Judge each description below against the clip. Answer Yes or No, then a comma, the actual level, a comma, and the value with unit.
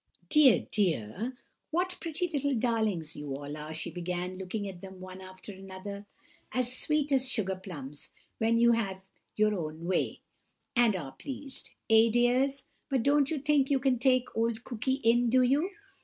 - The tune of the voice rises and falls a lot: Yes, wide, 5.9 semitones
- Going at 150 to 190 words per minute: Yes, average, 170 wpm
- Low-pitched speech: No, high, 225 Hz